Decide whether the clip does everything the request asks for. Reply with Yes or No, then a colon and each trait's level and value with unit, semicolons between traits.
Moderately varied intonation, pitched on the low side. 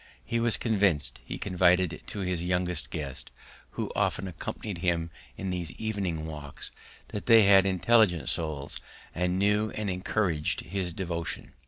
Yes: average, 3.2 semitones; very low, 90 Hz